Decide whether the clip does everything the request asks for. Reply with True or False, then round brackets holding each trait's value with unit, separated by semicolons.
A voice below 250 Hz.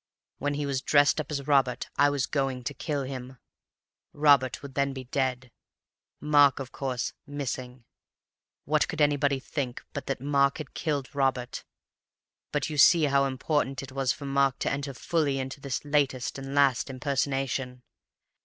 True (140 Hz)